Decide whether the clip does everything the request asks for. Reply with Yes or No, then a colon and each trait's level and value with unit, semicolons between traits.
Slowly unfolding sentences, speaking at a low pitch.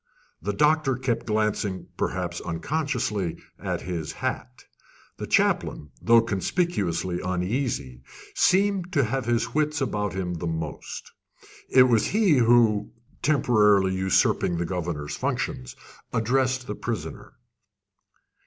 Yes: slow, 110 wpm; low, 110 Hz